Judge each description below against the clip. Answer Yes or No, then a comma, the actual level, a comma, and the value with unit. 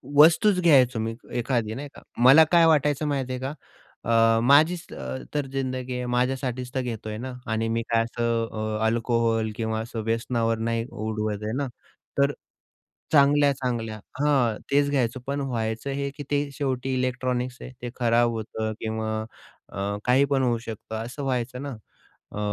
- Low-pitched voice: Yes, low, 125 Hz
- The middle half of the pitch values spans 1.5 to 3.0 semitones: No, average, 3.5 semitones